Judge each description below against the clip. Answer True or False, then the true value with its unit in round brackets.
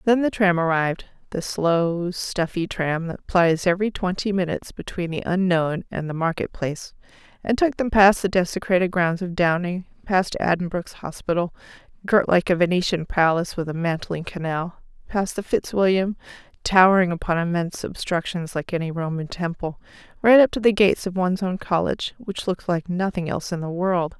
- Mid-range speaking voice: True (180 Hz)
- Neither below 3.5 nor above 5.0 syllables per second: False (5.4 syllables/s)